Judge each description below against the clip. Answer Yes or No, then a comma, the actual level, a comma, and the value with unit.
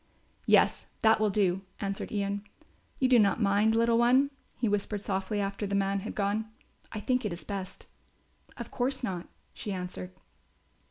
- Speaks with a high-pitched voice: Yes, high, 205 Hz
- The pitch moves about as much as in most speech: No, narrow, 2.3 semitones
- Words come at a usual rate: Yes, average, 165 wpm